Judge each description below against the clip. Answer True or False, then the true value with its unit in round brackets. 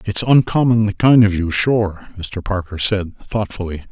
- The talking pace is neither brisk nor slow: True (155 wpm)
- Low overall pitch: True (100 Hz)